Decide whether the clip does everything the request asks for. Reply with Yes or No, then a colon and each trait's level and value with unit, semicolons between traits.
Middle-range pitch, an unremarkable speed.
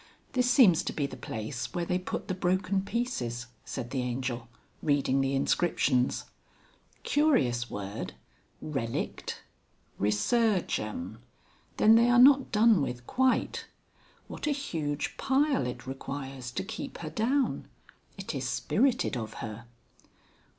No: medium, 145 Hz; slow, 130 wpm